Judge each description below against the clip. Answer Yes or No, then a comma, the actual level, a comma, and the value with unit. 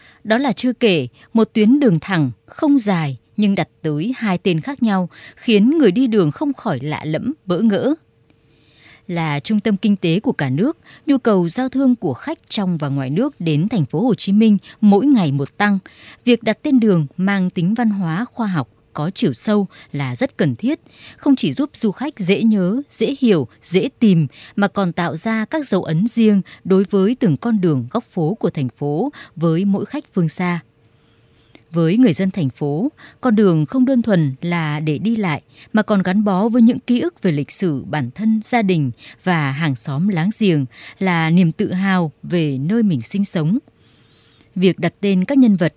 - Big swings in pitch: Yes, wide, 6.2 semitones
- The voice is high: Yes, high, 195 Hz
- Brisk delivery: No, average, 205 wpm